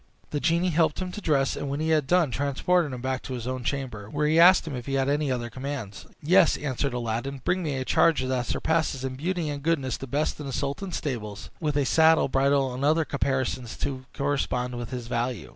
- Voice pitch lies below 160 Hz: Yes, medium, 140 Hz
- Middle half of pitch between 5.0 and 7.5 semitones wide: No, average, 3.3 semitones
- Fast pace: Yes, fast, 230 wpm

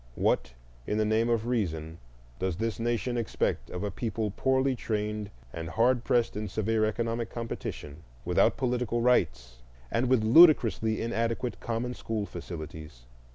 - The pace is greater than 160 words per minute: No, average, 145 wpm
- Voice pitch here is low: Yes, low, 110 Hz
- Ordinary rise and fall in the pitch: Yes, average, 3.3 semitones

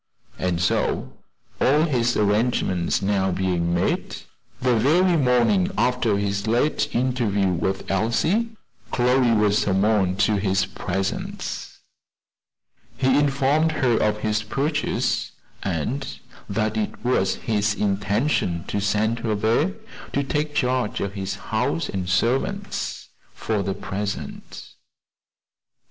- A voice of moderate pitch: No, low, 110 Hz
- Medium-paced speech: No, slow, 115 wpm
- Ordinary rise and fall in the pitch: Yes, average, 4.7 semitones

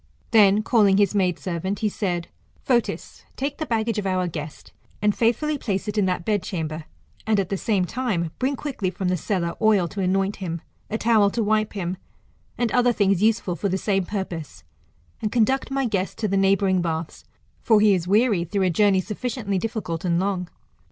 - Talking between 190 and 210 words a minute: Yes, average, 195 wpm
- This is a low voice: No, high, 200 Hz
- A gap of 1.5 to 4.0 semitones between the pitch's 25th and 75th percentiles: Yes, average, 3.2 semitones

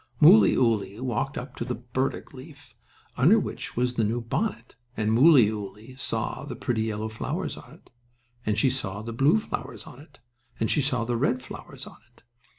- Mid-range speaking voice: No, low, 125 Hz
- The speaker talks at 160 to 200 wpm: Yes, average, 180 wpm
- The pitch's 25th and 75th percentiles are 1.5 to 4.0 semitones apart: Yes, average, 3.6 semitones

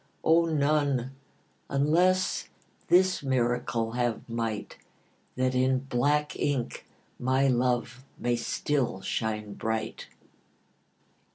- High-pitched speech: No, low, 130 Hz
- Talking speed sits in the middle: No, slow, 90 wpm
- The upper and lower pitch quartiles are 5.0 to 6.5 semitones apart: No, average, 3.3 semitones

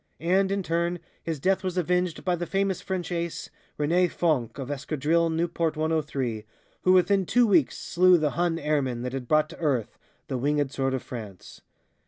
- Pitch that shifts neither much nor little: Yes, average, 4.1 semitones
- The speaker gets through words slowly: No, average, 180 wpm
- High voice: No, medium, 165 Hz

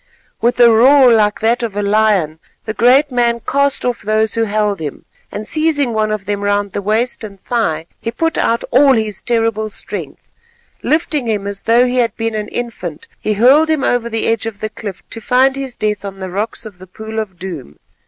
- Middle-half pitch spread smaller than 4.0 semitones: Yes, average, 2.9 semitones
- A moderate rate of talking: No, fast, 210 wpm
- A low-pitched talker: No, high, 220 Hz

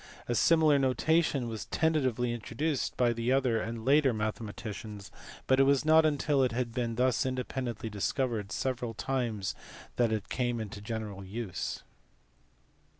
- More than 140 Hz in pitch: No, low, 120 Hz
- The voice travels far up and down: No, average, 3.3 semitones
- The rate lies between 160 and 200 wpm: No, average, 145 wpm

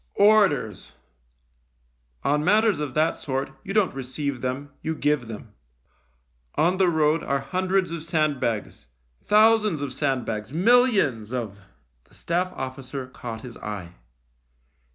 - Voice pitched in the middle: Yes, medium, 145 Hz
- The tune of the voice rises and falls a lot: Yes, wide, 6.3 semitones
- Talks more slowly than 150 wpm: Yes, slow, 135 wpm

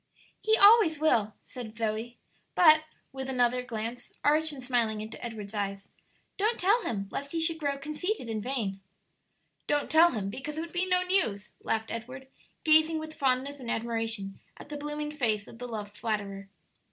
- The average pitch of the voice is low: No, very high, 255 Hz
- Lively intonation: Yes, wide, 6.0 semitones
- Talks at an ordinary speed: Yes, average, 175 wpm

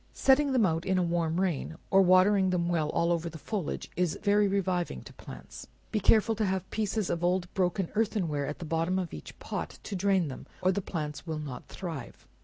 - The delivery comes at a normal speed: No, fast, 215 wpm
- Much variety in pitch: No, average, 3.0 semitones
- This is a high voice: No, medium, 180 Hz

